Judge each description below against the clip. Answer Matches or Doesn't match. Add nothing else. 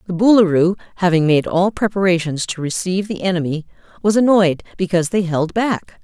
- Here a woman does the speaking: Matches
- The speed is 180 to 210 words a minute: Doesn't match